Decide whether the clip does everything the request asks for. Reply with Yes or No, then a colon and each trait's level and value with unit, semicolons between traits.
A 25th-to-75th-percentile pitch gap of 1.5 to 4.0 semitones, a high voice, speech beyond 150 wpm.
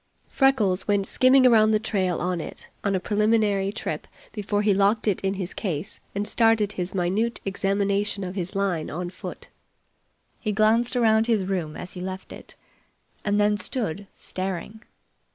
Yes: narrow, 2.5 semitones; high, 200 Hz; average, 165 wpm